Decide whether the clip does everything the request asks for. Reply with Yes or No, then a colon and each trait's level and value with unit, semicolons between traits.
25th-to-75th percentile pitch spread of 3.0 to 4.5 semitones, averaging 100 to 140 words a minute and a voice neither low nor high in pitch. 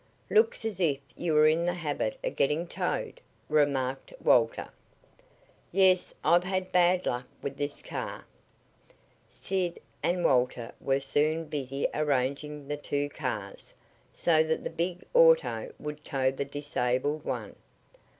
Yes: average, 4.2 semitones; slow, 135 wpm; medium, 150 Hz